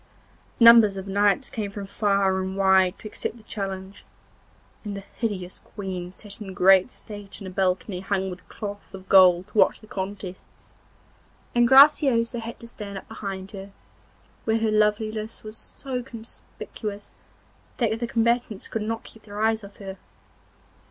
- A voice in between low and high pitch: No, high, 205 Hz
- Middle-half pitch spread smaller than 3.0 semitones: Yes, narrow, 2.6 semitones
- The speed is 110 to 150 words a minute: No, average, 160 wpm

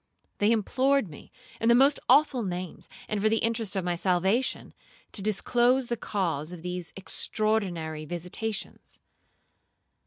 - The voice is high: Yes, high, 205 Hz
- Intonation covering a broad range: No, average, 4.9 semitones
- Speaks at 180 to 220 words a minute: No, slow, 135 wpm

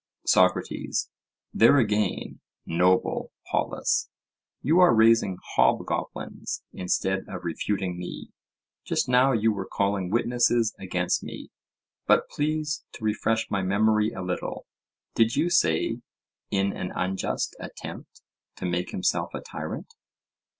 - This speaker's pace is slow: Yes, slow, 115 wpm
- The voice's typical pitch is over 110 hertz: No, low, 105 Hz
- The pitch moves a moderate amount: Yes, average, 3.8 semitones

